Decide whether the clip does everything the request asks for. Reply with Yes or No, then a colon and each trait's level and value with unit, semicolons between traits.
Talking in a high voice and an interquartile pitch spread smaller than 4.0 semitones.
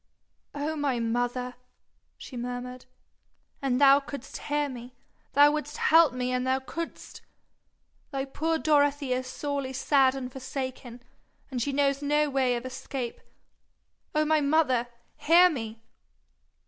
Yes: very high, 270 Hz; narrow, 2.5 semitones